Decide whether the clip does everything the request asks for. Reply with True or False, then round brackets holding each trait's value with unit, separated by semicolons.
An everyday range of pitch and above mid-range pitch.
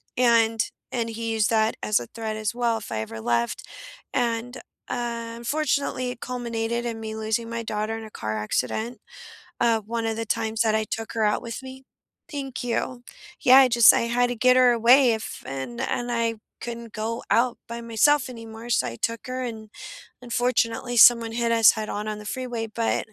False (1.7 semitones; 230 Hz)